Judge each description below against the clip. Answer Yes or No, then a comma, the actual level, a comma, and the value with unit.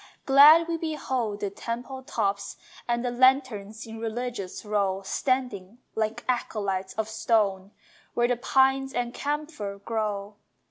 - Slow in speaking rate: Yes, slow, 130 wpm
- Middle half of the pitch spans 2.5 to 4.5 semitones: Yes, average, 4.2 semitones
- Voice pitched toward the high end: Yes, high, 230 Hz